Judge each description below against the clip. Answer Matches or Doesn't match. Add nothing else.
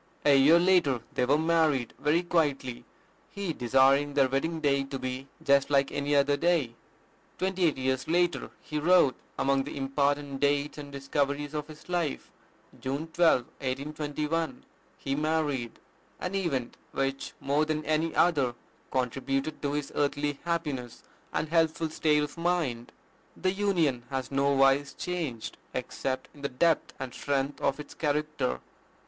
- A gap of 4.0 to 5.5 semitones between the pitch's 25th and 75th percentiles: Doesn't match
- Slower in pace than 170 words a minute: Matches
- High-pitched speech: Doesn't match